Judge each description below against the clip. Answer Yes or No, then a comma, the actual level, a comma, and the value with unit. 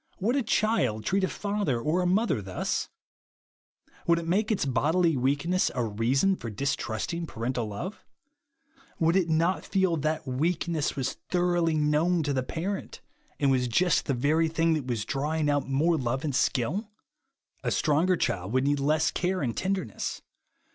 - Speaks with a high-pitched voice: No, medium, 155 Hz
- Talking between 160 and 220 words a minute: Yes, average, 175 wpm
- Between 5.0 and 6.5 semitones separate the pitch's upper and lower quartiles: Yes, average, 5.3 semitones